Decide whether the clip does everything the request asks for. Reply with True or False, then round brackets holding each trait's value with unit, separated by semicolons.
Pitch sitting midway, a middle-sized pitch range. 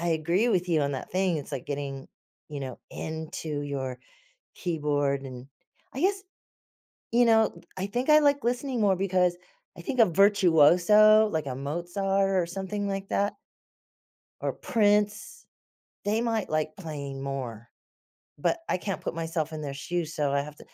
False (175 Hz; 6.1 semitones)